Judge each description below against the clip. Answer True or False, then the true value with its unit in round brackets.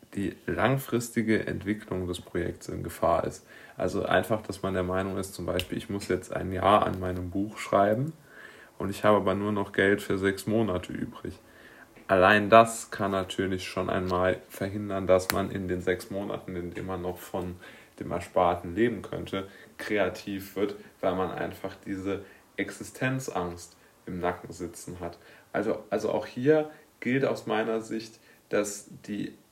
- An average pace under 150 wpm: False (165 wpm)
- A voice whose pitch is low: True (100 Hz)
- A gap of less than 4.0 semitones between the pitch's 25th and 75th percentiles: True (3.3 semitones)